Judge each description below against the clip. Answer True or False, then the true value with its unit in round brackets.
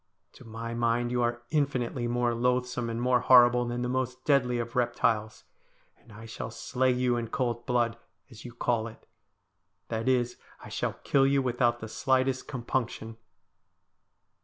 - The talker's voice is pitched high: False (120 Hz)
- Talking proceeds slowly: False (160 wpm)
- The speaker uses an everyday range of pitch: False (1.3 semitones)